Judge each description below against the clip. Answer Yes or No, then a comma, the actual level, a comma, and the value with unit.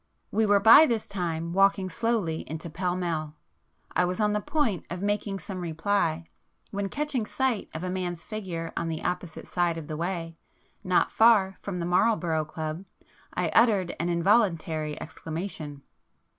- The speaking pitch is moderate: Yes, medium, 180 Hz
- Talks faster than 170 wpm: No, average, 160 wpm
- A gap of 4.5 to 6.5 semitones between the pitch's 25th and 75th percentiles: No, average, 3.8 semitones